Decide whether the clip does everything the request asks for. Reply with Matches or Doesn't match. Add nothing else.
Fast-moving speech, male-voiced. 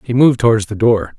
Matches